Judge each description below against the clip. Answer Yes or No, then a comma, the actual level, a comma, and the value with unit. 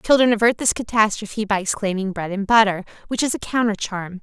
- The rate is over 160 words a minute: Yes, average, 200 wpm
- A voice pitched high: Yes, high, 210 Hz